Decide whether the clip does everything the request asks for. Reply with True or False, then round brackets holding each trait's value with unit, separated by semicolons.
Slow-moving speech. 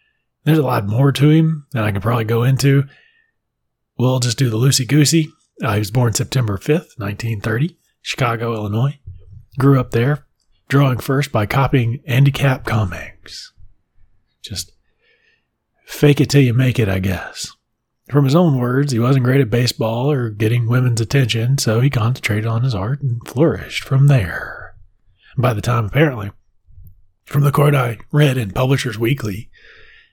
False (160 wpm)